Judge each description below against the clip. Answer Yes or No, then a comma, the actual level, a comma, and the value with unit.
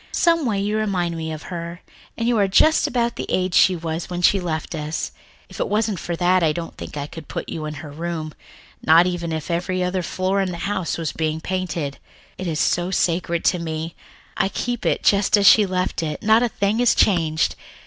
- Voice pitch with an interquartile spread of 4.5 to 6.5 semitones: No, average, 3.4 semitones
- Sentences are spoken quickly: Yes, fast, 220 wpm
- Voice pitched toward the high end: No, medium, 175 Hz